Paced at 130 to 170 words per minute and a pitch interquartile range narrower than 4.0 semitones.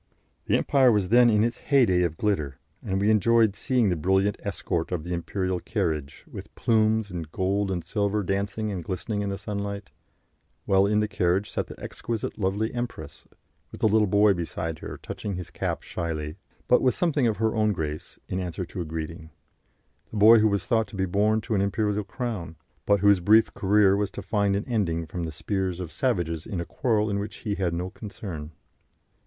No: fast, 205 wpm; average, 3.4 semitones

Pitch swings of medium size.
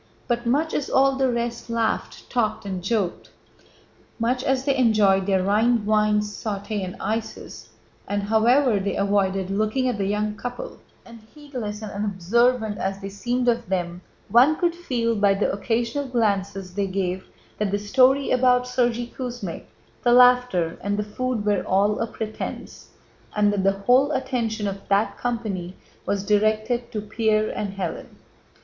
Yes: average, 3.5 semitones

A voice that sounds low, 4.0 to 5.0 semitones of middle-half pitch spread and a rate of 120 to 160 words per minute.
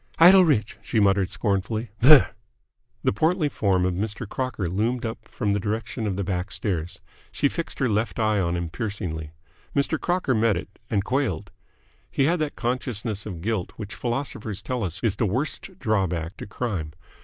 No: low, 110 Hz; average, 4.7 semitones; average, 175 wpm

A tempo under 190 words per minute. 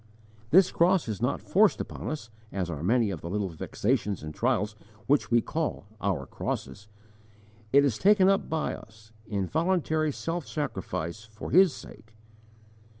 Yes: average, 155 wpm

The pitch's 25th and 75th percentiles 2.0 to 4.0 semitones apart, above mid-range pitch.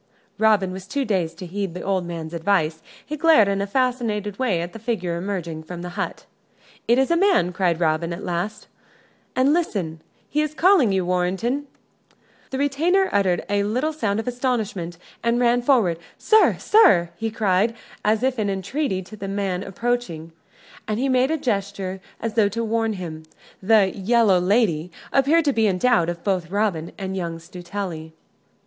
No: average, 5.3 semitones; high, 200 Hz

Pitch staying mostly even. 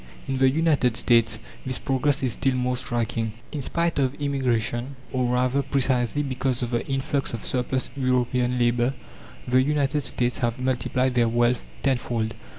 Yes: narrow, 2.0 semitones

